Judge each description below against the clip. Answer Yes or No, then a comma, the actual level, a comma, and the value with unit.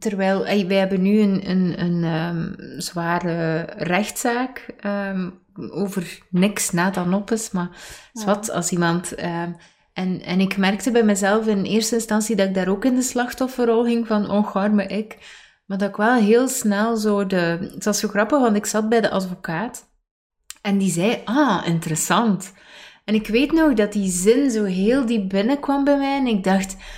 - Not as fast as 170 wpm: No, average, 185 wpm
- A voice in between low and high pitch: No, high, 205 Hz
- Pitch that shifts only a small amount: No, average, 3.4 semitones